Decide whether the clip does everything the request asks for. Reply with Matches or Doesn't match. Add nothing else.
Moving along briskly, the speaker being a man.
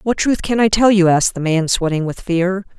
Doesn't match